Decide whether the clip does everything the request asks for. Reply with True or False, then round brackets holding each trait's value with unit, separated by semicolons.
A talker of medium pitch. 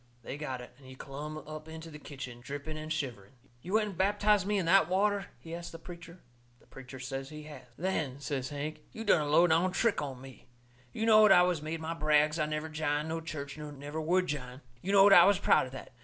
True (155 Hz)